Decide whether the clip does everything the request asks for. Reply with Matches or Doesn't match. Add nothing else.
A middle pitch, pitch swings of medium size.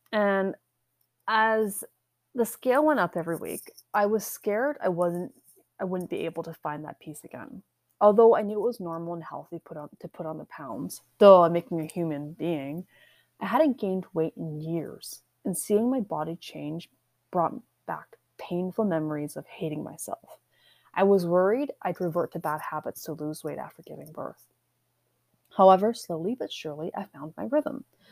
Matches